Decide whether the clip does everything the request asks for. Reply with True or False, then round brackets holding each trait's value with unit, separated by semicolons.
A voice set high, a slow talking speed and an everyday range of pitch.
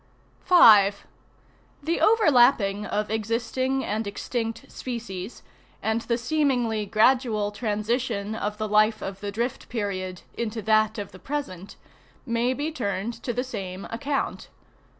True (220 Hz; 130 wpm; 3.3 semitones)